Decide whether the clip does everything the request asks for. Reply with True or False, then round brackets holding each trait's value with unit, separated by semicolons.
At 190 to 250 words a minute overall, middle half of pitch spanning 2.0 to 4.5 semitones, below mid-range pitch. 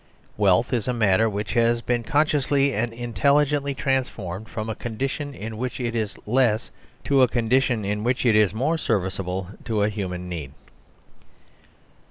False (160 wpm; 3.9 semitones; 115 Hz)